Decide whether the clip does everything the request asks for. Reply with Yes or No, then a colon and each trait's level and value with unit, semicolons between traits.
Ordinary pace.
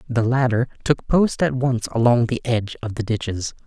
Yes: average, 195 wpm